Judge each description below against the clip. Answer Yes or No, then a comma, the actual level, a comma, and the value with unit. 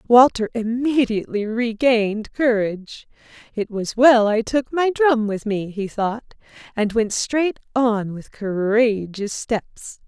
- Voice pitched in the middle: No, high, 225 Hz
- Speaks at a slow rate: Yes, slow, 130 wpm